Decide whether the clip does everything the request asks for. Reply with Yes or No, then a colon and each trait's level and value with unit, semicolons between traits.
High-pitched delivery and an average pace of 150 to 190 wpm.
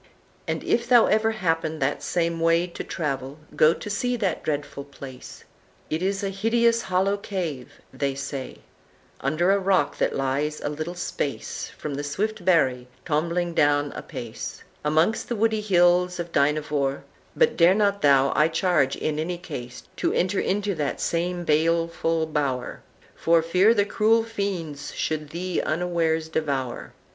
No: medium, 165 Hz; average, 155 wpm